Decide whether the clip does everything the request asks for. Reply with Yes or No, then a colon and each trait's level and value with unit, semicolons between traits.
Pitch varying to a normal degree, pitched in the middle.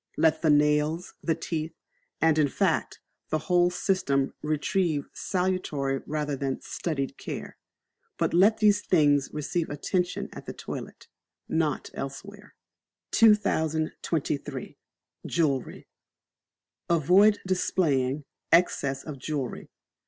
Yes: average, 3.9 semitones; medium, 155 Hz